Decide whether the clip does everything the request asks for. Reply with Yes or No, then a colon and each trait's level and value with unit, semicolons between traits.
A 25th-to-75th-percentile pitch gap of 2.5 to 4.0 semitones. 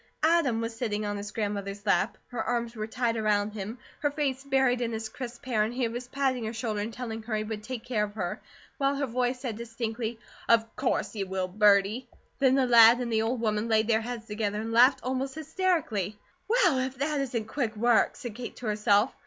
Yes: average, 2.9 semitones